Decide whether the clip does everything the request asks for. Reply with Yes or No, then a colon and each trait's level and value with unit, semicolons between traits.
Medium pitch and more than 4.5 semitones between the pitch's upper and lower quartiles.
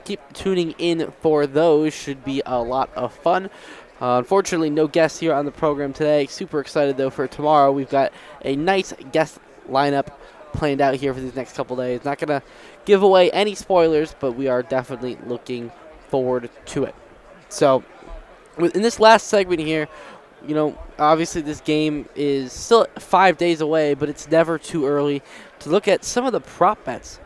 No: medium, 150 Hz; average, 3.3 semitones